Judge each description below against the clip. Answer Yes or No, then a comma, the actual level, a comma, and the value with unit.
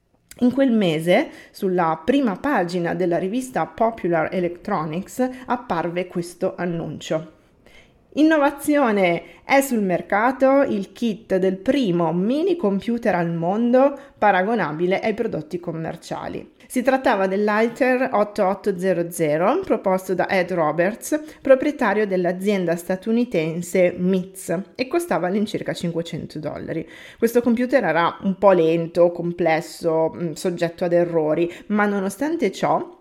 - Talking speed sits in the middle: No, slow, 105 wpm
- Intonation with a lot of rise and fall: Yes, wide, 6.3 semitones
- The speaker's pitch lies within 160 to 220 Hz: Yes, high, 190 Hz